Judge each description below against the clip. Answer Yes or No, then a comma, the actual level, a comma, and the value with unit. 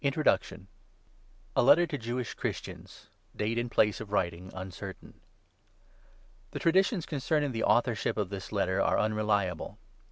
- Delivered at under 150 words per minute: Yes, slow, 135 wpm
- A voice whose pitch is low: Yes, low, 110 Hz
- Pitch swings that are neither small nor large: No, wide, 5.9 semitones